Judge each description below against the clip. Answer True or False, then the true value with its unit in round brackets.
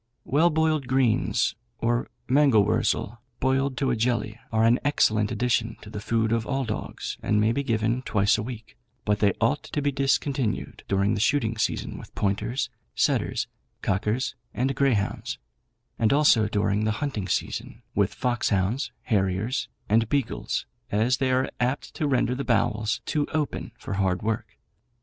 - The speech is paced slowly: False (160 wpm)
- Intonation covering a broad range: False (3.9 semitones)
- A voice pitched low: True (115 Hz)